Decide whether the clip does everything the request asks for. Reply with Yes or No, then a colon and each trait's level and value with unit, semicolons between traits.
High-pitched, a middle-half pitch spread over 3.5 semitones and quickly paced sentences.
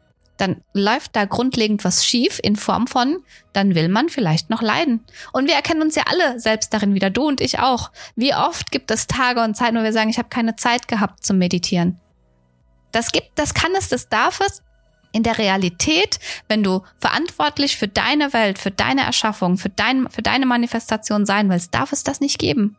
Yes: high, 225 Hz; average, 4.5 semitones; fast, 205 wpm